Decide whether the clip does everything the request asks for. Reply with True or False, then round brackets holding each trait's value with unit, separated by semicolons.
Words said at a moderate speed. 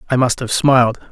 False (215 wpm)